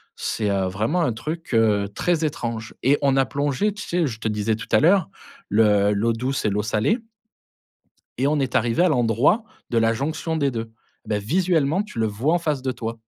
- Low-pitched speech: Yes, low, 125 Hz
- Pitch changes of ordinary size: No, wide, 5.9 semitones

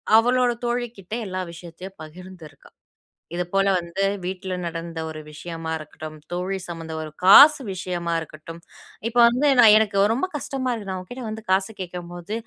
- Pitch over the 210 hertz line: No, medium, 185 Hz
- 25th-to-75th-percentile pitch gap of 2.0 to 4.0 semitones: No, average, 4.5 semitones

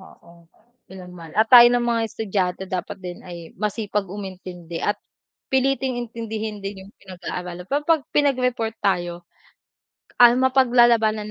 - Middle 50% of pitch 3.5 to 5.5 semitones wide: Yes, average, 4.9 semitones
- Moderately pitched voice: No, high, 210 Hz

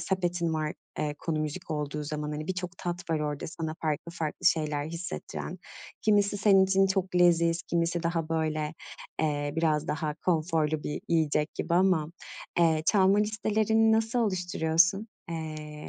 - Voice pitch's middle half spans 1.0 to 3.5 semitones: Yes, average, 3.2 semitones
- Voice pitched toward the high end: No, medium, 165 Hz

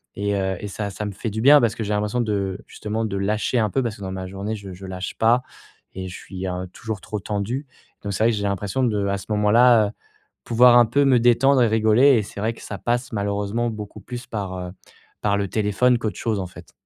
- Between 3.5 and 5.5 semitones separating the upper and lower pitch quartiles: No, average, 2.9 semitones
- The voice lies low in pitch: Yes, low, 105 Hz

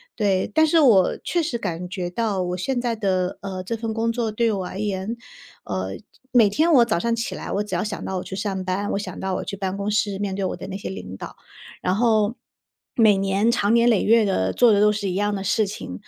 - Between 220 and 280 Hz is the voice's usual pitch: No, high, 205 Hz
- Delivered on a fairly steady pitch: No, average, 3.3 semitones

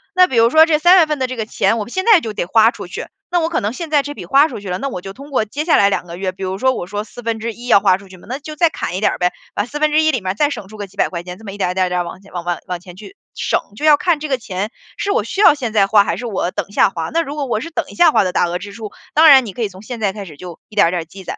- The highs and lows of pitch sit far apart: Yes, wide, 7.5 semitones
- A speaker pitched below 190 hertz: No, high, 220 Hz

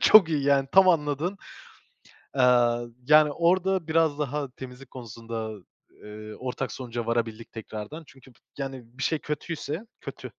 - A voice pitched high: No, low, 135 Hz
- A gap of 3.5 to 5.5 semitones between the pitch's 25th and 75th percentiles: Yes, average, 4.7 semitones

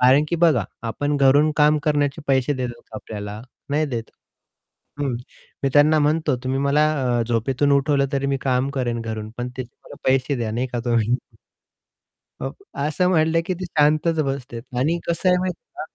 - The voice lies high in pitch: No, medium, 140 Hz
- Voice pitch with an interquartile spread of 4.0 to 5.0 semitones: No, average, 3.6 semitones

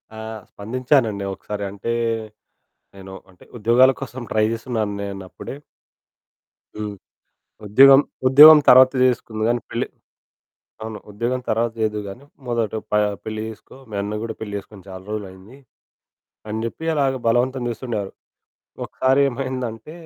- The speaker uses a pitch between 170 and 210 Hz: No, low, 115 Hz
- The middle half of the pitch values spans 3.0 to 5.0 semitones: Yes, average, 3.6 semitones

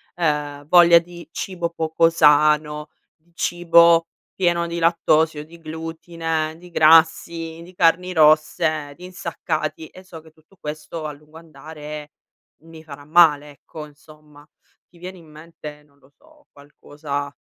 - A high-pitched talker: No, medium, 160 Hz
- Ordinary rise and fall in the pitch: No, narrow, 2.0 semitones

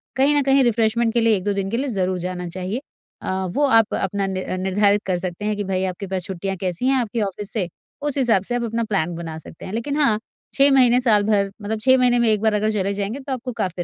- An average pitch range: Yes, average, 4.0 semitones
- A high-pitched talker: Yes, high, 210 Hz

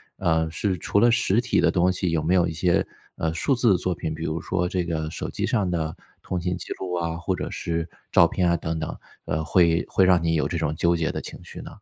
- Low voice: Yes, very low, 85 Hz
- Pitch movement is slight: Yes, narrow, 2.2 semitones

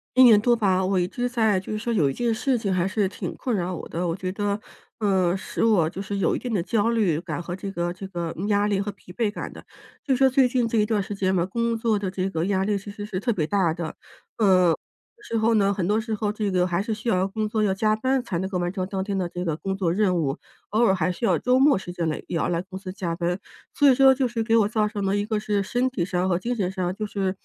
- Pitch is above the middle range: Yes, high, 200 Hz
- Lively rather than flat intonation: No, average, 3.2 semitones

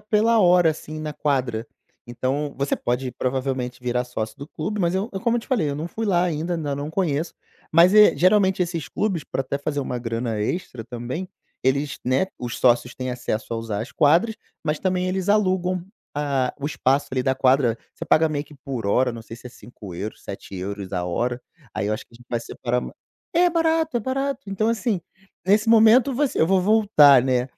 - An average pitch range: No, wide, 7.3 semitones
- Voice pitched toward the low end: No, medium, 145 Hz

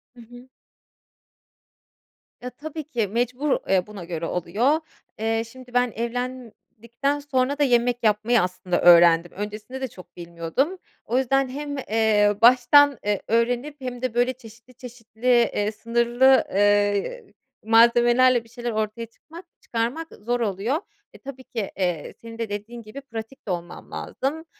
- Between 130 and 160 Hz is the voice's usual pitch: No, high, 235 Hz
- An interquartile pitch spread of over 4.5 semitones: No, average, 3.4 semitones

